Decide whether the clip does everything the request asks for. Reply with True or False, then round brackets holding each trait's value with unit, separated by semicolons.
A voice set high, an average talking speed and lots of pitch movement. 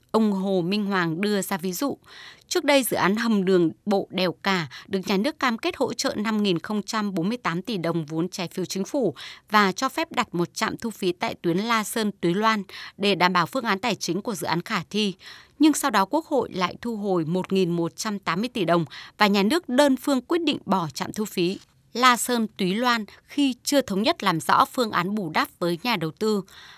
False (200 Hz; 220 wpm; 4.8 semitones)